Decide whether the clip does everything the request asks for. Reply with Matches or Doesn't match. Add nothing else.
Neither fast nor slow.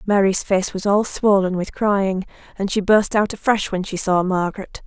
Matches